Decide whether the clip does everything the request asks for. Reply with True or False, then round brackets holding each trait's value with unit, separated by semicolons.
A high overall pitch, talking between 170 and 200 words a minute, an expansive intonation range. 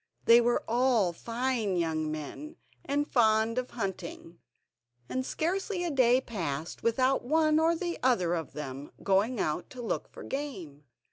False (230 Hz; 145 wpm; 7.2 semitones)